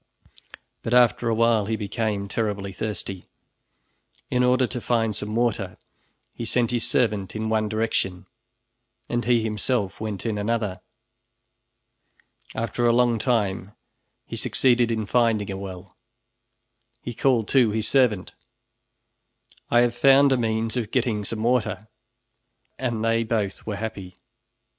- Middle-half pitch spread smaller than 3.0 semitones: Yes, narrow, 2.4 semitones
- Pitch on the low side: Yes, low, 110 Hz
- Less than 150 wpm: Yes, slow, 135 wpm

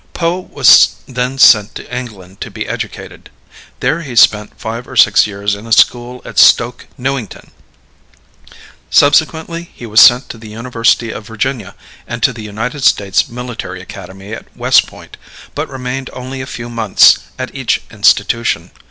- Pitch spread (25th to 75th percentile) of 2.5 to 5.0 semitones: Yes, average, 3.4 semitones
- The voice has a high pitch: No, low, 120 Hz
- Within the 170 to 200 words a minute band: No, average, 160 wpm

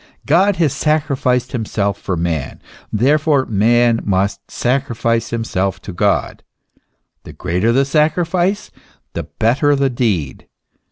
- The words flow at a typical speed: No, slow, 115 wpm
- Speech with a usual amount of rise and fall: No, wide, 6.1 semitones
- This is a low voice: Yes, low, 120 Hz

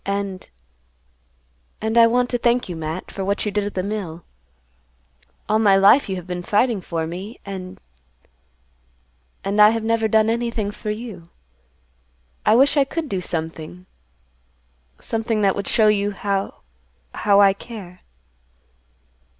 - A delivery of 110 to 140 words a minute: Yes, slow, 135 wpm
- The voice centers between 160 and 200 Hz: Yes, high, 190 Hz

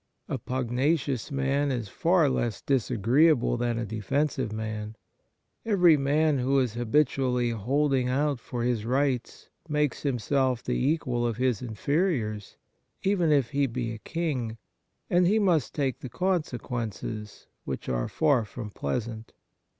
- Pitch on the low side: Yes, low, 130 Hz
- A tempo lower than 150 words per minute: Yes, average, 140 wpm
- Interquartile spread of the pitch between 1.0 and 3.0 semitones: No, average, 4.2 semitones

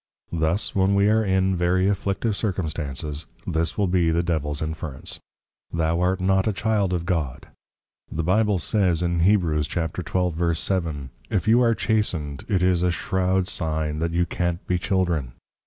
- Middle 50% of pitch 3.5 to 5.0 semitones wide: No, average, 2.9 semitones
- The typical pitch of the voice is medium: No, very low, 90 Hz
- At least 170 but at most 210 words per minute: No, average, 160 wpm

